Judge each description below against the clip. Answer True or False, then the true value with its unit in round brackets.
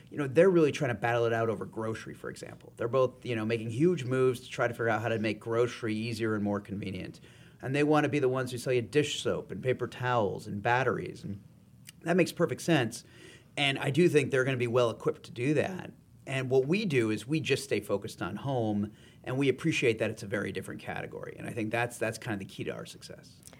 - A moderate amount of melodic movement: True (4.0 semitones)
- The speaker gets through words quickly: True (255 wpm)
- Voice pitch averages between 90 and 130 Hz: True (125 Hz)